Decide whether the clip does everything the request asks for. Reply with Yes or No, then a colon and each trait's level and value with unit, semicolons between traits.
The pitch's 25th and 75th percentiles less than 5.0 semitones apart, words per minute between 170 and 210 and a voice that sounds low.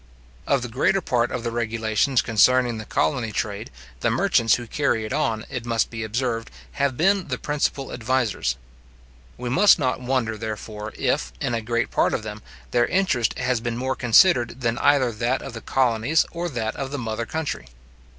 Yes: average, 2.8 semitones; average, 185 wpm; low, 120 Hz